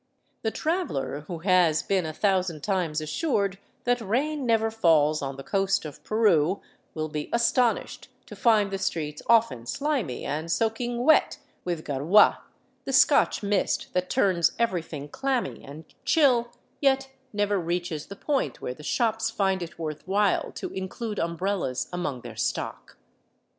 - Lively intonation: Yes, wide, 6.4 semitones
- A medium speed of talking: Yes, average, 150 wpm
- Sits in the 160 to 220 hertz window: Yes, high, 190 Hz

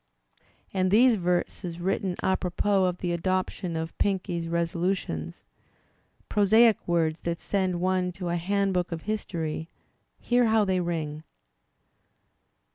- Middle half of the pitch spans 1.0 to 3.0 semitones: Yes, narrow, 2.4 semitones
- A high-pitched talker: No, medium, 180 Hz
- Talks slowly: Yes, slow, 120 wpm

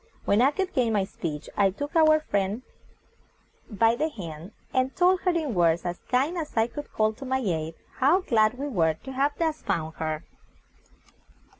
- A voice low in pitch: No, high, 235 Hz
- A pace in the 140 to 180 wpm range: No, average, 190 wpm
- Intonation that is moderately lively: No, wide, 7.9 semitones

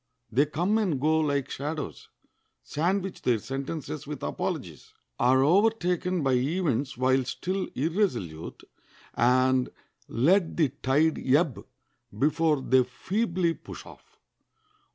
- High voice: No, medium, 150 Hz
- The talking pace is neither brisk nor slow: No, slow, 110 wpm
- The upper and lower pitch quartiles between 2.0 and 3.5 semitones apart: No, average, 5.1 semitones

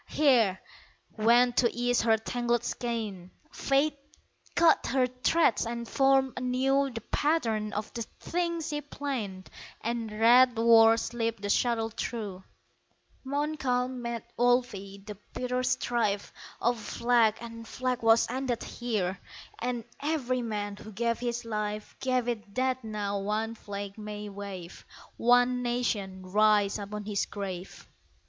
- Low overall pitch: No, high, 235 Hz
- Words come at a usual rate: No, slow, 130 wpm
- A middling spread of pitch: Yes, average, 3.1 semitones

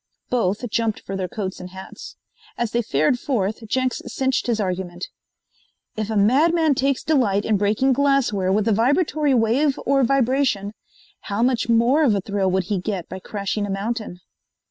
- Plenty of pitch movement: No, average, 4.9 semitones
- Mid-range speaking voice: No, high, 220 Hz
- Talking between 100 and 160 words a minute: No, average, 170 wpm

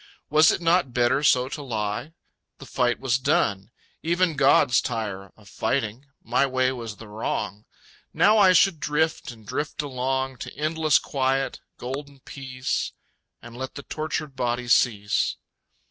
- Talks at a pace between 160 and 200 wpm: No, average, 145 wpm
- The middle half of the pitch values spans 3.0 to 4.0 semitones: Yes, average, 3.7 semitones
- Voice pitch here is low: Yes, low, 130 Hz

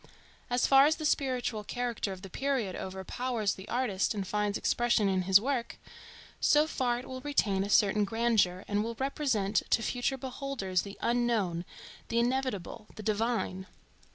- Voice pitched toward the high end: Yes, high, 230 Hz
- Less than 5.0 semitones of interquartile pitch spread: Yes, average, 4.3 semitones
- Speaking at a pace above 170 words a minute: No, average, 160 wpm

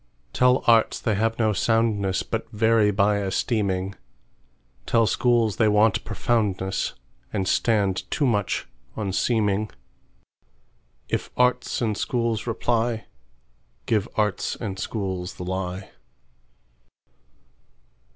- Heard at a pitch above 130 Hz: No, low, 105 Hz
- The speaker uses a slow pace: Yes, slow, 90 wpm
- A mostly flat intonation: No, average, 3.1 semitones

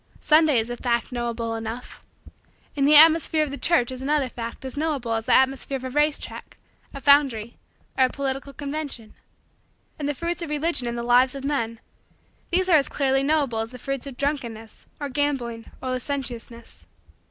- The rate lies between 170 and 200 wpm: Yes, average, 185 wpm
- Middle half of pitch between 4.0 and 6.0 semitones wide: No, average, 3.6 semitones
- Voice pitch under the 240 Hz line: No, very high, 270 Hz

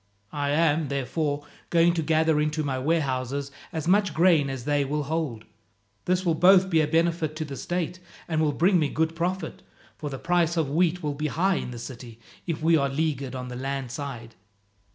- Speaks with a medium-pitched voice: Yes, medium, 155 Hz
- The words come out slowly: No, average, 200 wpm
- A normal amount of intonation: Yes, average, 3.2 semitones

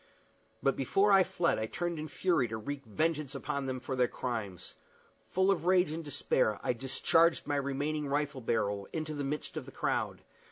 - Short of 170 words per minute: No, average, 190 wpm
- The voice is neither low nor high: Yes, medium, 145 Hz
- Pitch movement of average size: Yes, average, 4.3 semitones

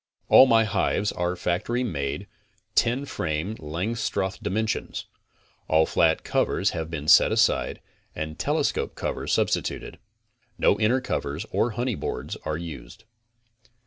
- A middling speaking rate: No, slow, 125 wpm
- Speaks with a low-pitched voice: Yes, very low, 90 Hz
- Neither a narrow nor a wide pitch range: No, wide, 6.0 semitones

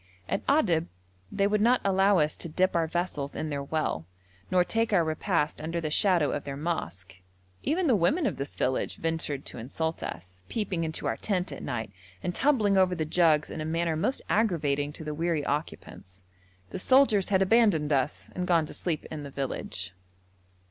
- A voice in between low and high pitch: Yes, medium, 165 Hz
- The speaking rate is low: No, average, 190 wpm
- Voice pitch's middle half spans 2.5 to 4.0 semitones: No, average, 4.6 semitones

